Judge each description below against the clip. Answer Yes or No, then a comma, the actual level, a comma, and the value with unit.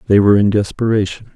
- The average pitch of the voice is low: Yes, low, 105 Hz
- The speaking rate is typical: Yes, average, 175 wpm